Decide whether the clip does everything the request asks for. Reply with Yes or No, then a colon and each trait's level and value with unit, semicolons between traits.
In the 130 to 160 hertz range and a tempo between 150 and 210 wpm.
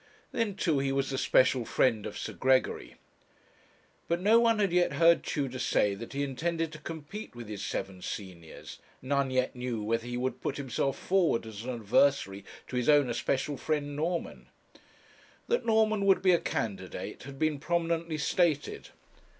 Yes: medium, 140 Hz; average, 170 wpm